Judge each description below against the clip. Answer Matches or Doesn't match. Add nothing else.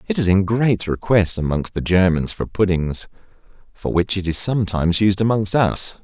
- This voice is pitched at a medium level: Doesn't match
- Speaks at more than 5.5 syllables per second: Doesn't match